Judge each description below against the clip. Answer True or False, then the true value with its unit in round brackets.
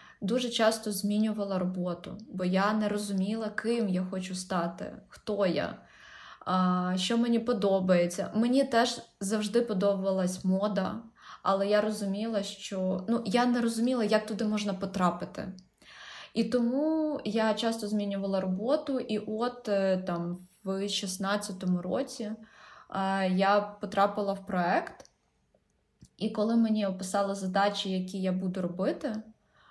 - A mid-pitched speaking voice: False (205 Hz)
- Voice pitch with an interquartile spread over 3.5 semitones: False (2.7 semitones)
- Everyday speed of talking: True (120 wpm)